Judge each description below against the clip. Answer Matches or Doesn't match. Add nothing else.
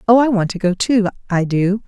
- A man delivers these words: Doesn't match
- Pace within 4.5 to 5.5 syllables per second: Matches